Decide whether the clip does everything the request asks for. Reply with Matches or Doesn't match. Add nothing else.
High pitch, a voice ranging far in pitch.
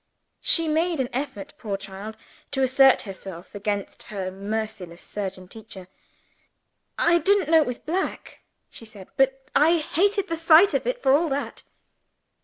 Matches